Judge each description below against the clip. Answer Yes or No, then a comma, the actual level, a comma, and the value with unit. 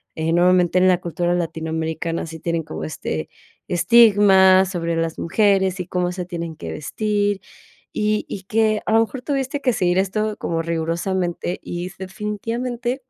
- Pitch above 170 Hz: Yes, medium, 185 Hz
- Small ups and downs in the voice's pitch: No, average, 3.8 semitones